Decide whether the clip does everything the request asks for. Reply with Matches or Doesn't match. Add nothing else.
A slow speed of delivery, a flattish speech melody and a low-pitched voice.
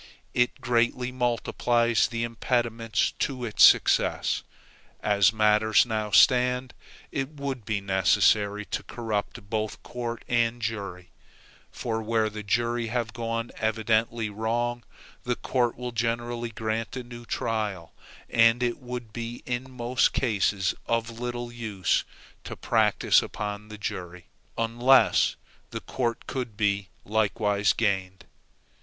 Matches